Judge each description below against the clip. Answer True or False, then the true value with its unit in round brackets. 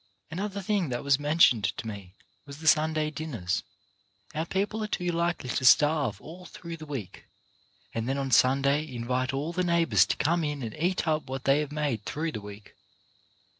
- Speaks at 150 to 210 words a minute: True (190 wpm)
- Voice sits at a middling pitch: True (145 Hz)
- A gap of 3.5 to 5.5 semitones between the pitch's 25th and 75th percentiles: True (4.6 semitones)